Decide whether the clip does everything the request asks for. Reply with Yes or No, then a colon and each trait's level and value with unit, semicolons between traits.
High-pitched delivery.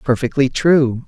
No: low, 135 Hz